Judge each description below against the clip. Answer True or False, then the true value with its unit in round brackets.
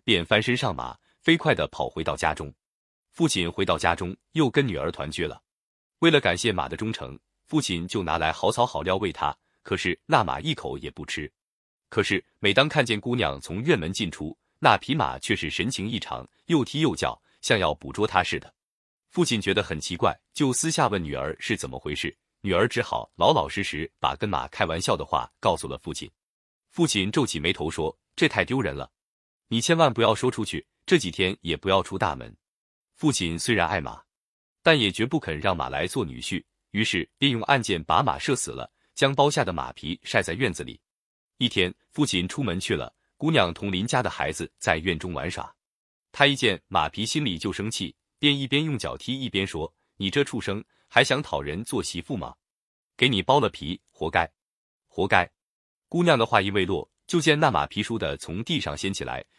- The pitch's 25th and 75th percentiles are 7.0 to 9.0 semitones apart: True (7.8 semitones)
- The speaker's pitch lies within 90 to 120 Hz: True (110 Hz)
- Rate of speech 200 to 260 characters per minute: False (280 characters per minute)